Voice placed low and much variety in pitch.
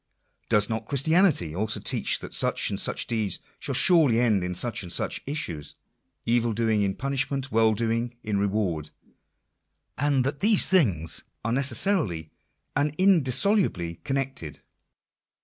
Yes: low, 115 Hz; wide, 5.8 semitones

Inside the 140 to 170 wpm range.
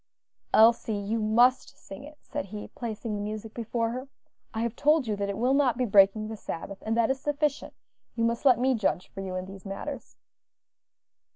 No: average, 200 wpm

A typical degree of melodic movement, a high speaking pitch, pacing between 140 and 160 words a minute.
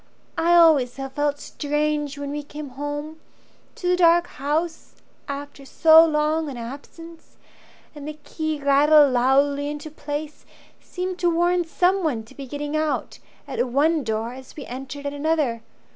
No: narrow, 2.3 semitones; very high, 295 Hz; average, 155 wpm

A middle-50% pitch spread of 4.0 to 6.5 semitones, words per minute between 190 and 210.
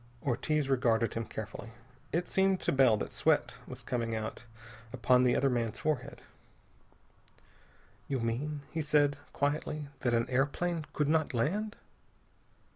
No: average, 4.4 semitones; slow, 135 wpm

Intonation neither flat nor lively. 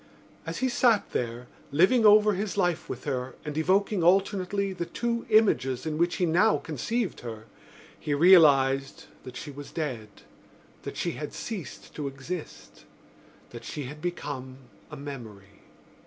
No: wide, 6.5 semitones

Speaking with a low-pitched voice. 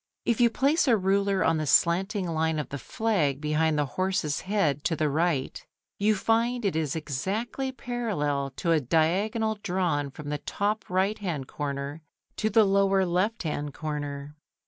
No: medium, 175 Hz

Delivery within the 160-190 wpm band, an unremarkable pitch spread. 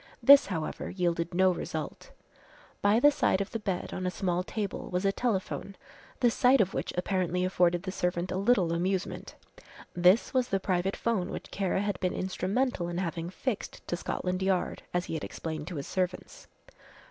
No: average, 180 wpm; narrow, 2.1 semitones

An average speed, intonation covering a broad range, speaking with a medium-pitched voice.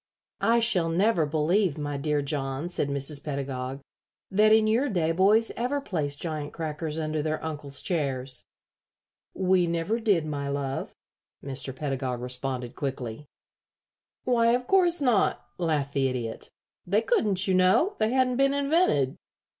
Yes: average, 145 wpm; wide, 7.4 semitones; medium, 160 Hz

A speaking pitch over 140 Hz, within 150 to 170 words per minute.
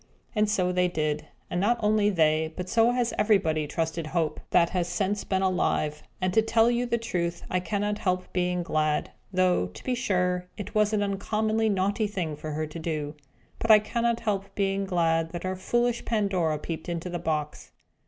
No: medium, 185 Hz; average, 195 wpm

